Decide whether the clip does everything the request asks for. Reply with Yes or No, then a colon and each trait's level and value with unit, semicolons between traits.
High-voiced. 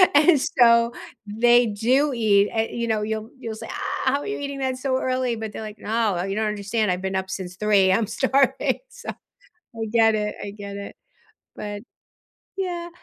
Yes: high, 225 Hz